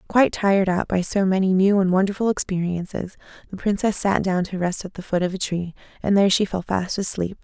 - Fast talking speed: Yes, fast, 225 wpm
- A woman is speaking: Yes, female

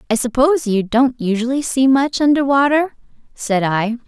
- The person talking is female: Yes, female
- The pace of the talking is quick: No, average, 160 wpm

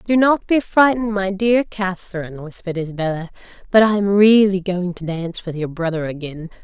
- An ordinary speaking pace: Yes, average, 180 wpm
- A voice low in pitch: No, high, 190 Hz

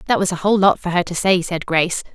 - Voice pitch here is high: No, medium, 180 Hz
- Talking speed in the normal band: No, fast, 305 wpm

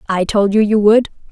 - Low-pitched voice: No, high, 210 Hz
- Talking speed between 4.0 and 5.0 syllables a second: No, 5.2 syllables/s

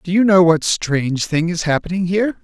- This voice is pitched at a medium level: Yes, medium, 175 Hz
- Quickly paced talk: Yes, fast, 220 wpm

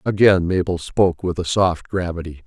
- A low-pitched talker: Yes, very low, 90 Hz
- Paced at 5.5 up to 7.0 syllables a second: No, 5.1 syllables/s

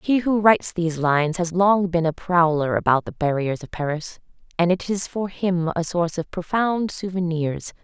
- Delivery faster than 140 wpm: Yes, average, 190 wpm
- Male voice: No, female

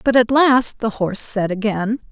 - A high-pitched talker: Yes, high, 225 Hz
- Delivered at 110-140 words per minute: No, average, 200 wpm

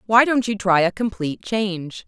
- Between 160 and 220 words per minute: Yes, fast, 205 wpm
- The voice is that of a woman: Yes, female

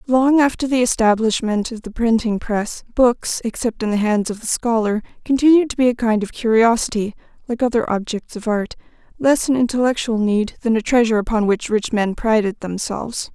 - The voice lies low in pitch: No, high, 230 Hz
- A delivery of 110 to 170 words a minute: No, average, 185 wpm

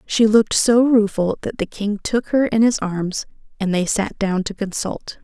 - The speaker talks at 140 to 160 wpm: No, fast, 205 wpm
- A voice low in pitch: No, high, 205 Hz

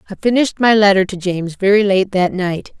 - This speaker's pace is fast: Yes, fast, 215 wpm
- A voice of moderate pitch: No, high, 195 Hz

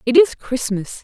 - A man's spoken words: No, female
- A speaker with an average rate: Yes, average, 175 wpm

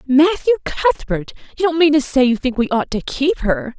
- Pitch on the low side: No, very high, 270 Hz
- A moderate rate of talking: No, fast, 220 wpm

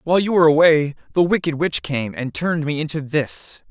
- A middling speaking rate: No, fast, 210 wpm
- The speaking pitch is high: No, medium, 155 Hz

